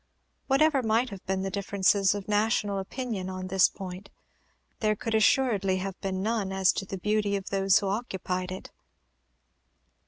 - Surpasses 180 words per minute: No, average, 160 wpm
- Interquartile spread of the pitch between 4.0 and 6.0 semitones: No, narrow, 2.4 semitones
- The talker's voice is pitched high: Yes, high, 200 Hz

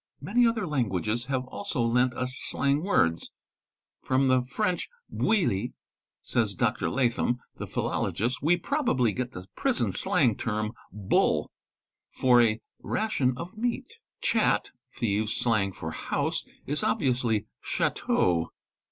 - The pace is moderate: No, slow, 125 wpm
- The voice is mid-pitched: No, low, 125 Hz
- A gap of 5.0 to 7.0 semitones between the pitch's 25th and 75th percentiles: Yes, wide, 5.5 semitones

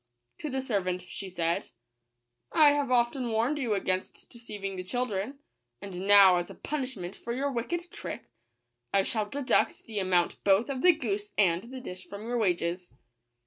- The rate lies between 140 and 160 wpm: No, average, 180 wpm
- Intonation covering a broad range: Yes, wide, 5.9 semitones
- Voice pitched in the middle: No, high, 210 Hz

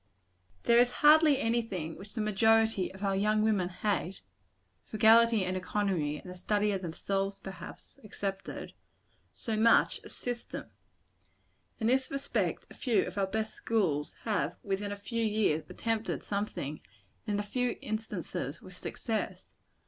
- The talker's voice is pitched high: Yes, high, 210 Hz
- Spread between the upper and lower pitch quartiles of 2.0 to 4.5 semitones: Yes, average, 2.8 semitones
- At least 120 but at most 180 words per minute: Yes, average, 150 wpm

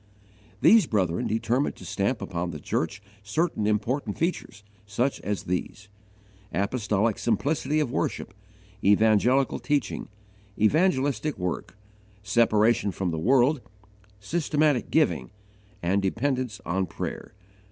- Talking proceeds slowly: Yes, slow, 110 wpm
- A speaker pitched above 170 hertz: No, low, 110 Hz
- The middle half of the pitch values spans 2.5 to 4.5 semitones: No, wide, 5.5 semitones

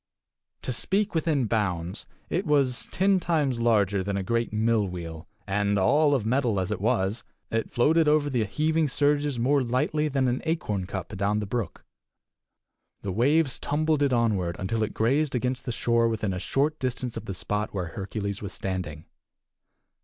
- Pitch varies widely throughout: Yes, wide, 6.1 semitones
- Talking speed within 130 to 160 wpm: No, average, 175 wpm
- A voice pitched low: Yes, low, 115 Hz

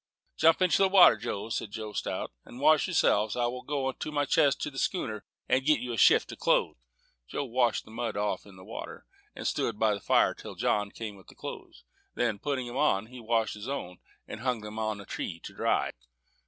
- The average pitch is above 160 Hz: No, low, 120 Hz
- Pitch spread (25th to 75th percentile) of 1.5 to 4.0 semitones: No, average, 4.6 semitones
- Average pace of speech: No, fast, 235 wpm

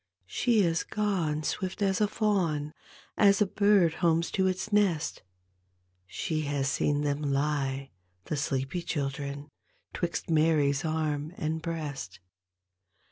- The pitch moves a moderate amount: Yes, average, 4.4 semitones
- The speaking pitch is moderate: Yes, medium, 155 Hz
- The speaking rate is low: Yes, slow, 125 wpm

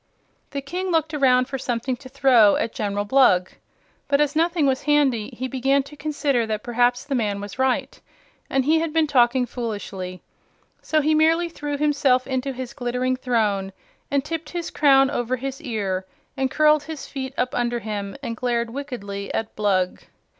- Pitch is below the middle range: No, very high, 260 Hz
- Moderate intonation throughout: Yes, average, 3.8 semitones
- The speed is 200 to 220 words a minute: No, average, 175 wpm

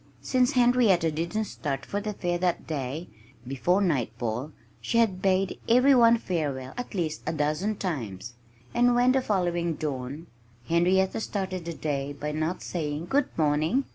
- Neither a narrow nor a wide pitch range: No, wide, 6.0 semitones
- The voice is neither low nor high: Yes, medium, 175 Hz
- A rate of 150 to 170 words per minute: Yes, average, 155 wpm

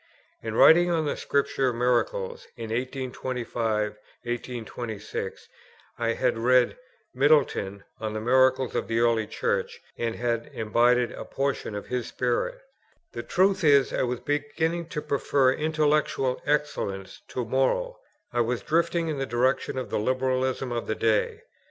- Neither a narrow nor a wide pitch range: Yes, average, 3.9 semitones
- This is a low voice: Yes, low, 130 Hz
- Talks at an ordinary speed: Yes, average, 145 wpm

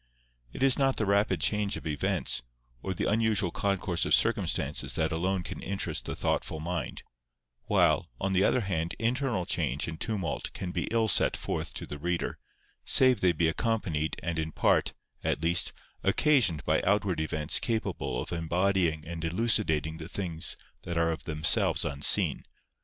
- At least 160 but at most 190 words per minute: Yes, average, 165 wpm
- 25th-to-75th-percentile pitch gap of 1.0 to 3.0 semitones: No, average, 4.3 semitones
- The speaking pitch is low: Yes, very low, 90 Hz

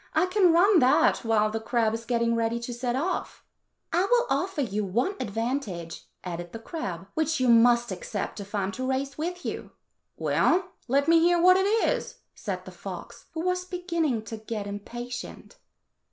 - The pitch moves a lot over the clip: Yes, wide, 7.5 semitones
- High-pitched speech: Yes, high, 245 Hz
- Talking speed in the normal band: Yes, average, 180 wpm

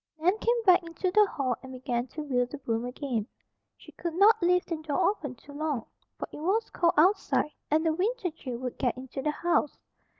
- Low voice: No, very high, 305 Hz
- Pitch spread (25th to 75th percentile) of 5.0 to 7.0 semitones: Yes, wide, 5.7 semitones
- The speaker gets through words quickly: Yes, fast, 210 wpm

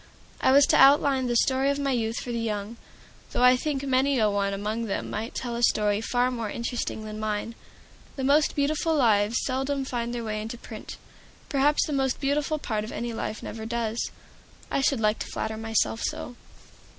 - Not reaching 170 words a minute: No, average, 200 wpm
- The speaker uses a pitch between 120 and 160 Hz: No, high, 240 Hz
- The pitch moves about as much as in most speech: Yes, average, 3.7 semitones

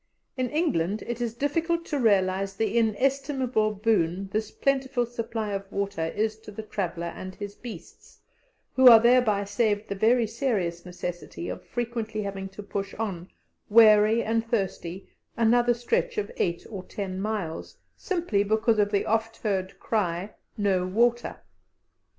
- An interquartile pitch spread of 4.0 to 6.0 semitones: No, average, 3.4 semitones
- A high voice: Yes, high, 215 Hz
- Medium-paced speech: Yes, average, 150 wpm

